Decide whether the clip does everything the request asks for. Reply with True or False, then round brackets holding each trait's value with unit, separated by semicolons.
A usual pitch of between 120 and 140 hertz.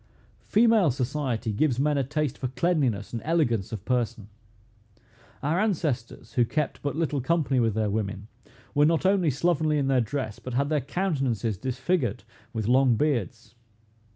True (135 Hz)